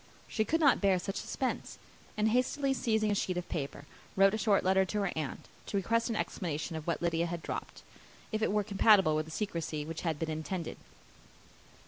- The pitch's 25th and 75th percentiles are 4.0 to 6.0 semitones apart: Yes, average, 4.8 semitones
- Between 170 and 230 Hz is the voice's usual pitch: Yes, high, 190 Hz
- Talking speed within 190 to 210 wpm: Yes, average, 200 wpm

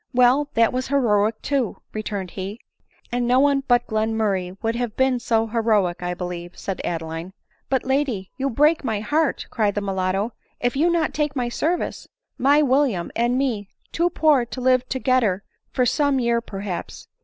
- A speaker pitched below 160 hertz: No, high, 240 Hz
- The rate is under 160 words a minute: No, average, 190 wpm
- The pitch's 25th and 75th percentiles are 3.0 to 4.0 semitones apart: No, average, 4.8 semitones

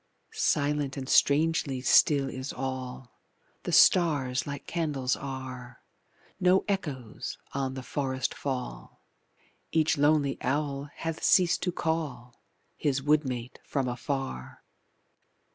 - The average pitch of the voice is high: No, medium, 140 Hz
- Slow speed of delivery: Yes, slow, 110 wpm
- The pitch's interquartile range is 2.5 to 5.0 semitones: Yes, average, 2.8 semitones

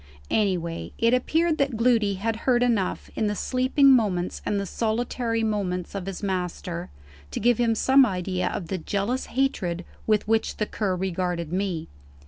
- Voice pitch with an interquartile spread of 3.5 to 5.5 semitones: Yes, average, 4.7 semitones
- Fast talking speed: No, average, 165 wpm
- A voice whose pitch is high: Yes, high, 210 Hz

